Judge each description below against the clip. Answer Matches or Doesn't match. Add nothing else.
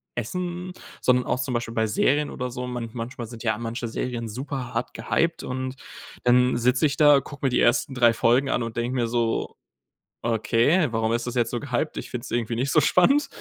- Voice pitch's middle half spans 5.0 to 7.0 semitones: Doesn't match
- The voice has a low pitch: Matches